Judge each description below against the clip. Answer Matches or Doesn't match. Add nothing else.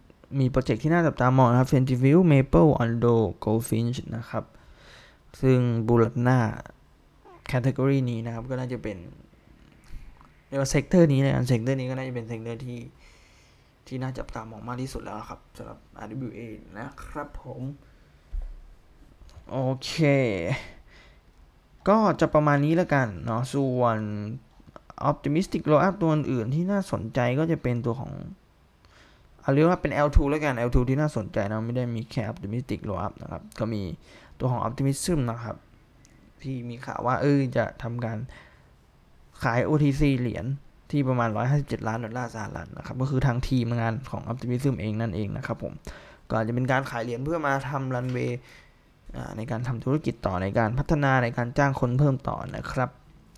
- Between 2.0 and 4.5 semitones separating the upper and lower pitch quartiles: Matches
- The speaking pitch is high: Doesn't match